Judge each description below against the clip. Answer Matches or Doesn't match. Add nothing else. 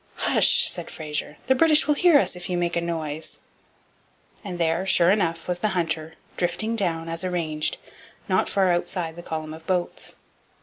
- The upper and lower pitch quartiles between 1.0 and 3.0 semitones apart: Matches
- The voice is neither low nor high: Matches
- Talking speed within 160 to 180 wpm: Matches